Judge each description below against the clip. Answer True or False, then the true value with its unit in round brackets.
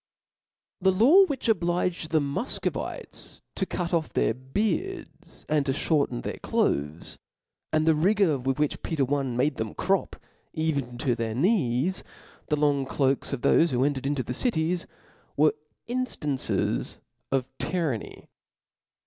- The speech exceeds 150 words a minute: False (135 wpm)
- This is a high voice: False (150 Hz)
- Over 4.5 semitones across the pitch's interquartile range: True (5.3 semitones)